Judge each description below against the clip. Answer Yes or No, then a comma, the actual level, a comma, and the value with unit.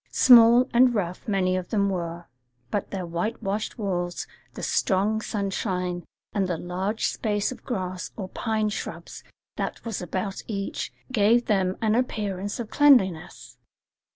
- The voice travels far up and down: No, average, 3.1 semitones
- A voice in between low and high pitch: No, high, 200 Hz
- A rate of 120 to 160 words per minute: Yes, average, 140 wpm